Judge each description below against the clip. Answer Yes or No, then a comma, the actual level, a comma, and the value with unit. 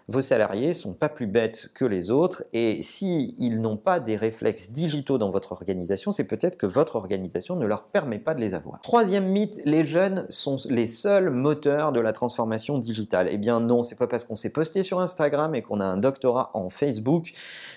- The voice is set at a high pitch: No, low, 135 Hz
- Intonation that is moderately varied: No, wide, 6.5 semitones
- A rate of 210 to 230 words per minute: Yes, average, 215 wpm